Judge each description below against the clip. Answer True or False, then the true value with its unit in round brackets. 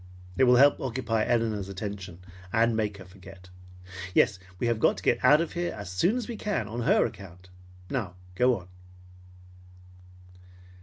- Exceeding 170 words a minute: False (165 wpm)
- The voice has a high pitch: False (110 Hz)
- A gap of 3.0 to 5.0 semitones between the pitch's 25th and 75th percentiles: True (4.7 semitones)